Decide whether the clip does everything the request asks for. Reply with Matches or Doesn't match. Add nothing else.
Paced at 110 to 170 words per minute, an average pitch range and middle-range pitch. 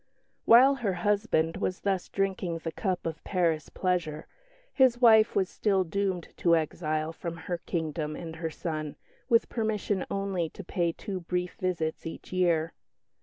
Matches